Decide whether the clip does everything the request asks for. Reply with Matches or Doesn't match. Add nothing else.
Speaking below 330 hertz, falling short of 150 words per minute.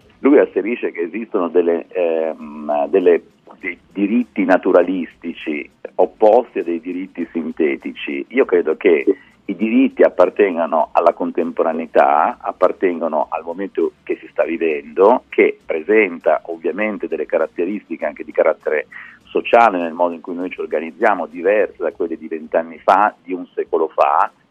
Doesn't match